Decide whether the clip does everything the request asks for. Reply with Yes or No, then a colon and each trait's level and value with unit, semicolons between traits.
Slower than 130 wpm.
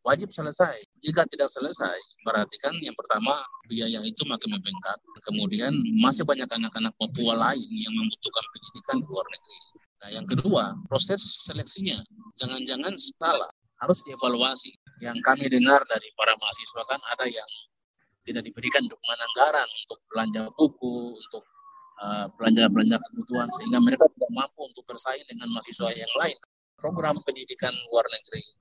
No: fast, 140 wpm